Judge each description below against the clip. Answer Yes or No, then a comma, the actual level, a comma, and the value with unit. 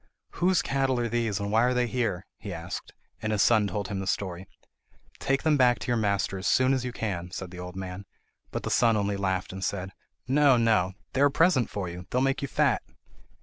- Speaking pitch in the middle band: No, low, 105 Hz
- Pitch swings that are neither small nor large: Yes, average, 4.9 semitones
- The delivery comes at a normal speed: No, fast, 235 wpm